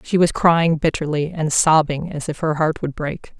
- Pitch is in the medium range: Yes, medium, 155 Hz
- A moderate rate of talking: No, fast, 210 wpm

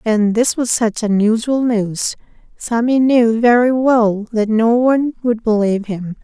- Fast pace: No, average, 155 wpm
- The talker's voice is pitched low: No, high, 230 Hz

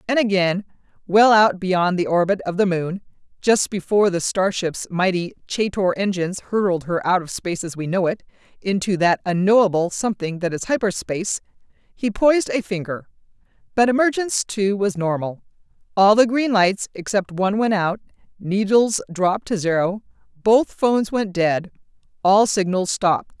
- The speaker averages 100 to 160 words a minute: Yes, average, 155 wpm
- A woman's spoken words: Yes, female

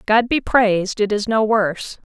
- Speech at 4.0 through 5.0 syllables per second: Yes, 4.7 syllables/s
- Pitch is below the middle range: No, high, 215 Hz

